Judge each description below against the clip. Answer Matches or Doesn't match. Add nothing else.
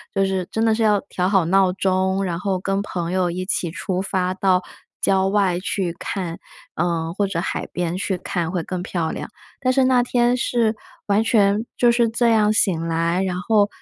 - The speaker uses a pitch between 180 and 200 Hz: Matches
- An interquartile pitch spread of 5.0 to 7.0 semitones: Doesn't match